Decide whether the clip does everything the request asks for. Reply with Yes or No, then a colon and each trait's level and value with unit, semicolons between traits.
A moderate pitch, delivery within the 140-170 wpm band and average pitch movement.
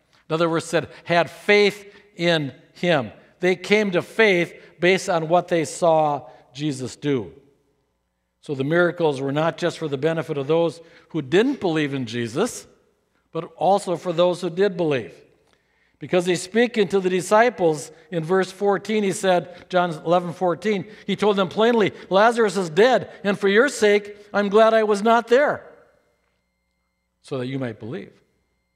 Yes: medium, 175 Hz; average, 165 wpm; average, 4.6 semitones